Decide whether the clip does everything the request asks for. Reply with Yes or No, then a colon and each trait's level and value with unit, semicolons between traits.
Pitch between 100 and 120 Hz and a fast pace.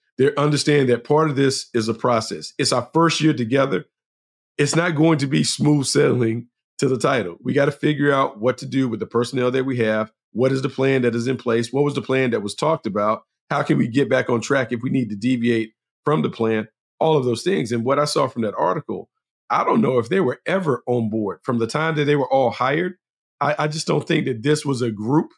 No: low, 130 Hz; fast, 255 wpm